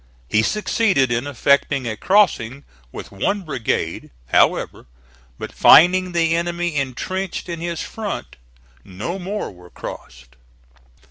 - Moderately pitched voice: Yes, medium, 165 Hz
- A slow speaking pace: Yes, slow, 120 wpm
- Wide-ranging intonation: Yes, wide, 7.8 semitones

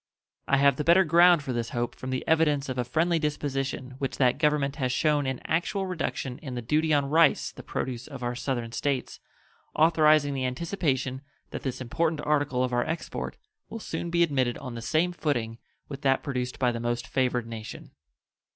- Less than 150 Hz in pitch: Yes, medium, 140 Hz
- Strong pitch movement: No, average, 3.8 semitones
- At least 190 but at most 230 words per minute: Yes, average, 195 wpm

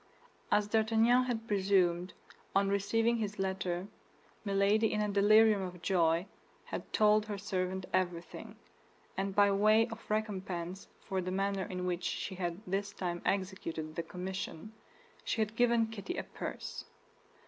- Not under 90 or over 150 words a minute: Yes, average, 145 wpm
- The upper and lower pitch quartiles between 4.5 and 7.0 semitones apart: No, average, 2.7 semitones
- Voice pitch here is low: No, high, 195 Hz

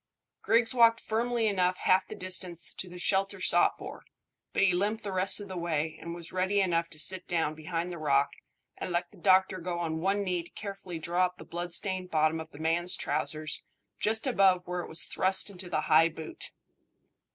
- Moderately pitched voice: Yes, medium, 180 Hz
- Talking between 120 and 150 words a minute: No, fast, 205 wpm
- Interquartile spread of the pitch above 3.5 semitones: No, average, 2.7 semitones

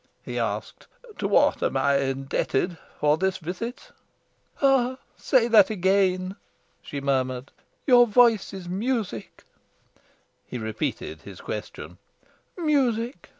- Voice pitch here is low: No, high, 190 Hz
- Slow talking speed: Yes, slow, 110 wpm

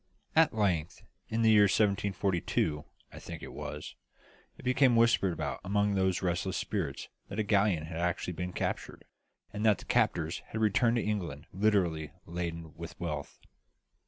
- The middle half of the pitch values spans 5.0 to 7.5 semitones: No, average, 4.1 semitones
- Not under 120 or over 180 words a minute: Yes, average, 160 wpm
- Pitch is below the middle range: Yes, very low, 95 Hz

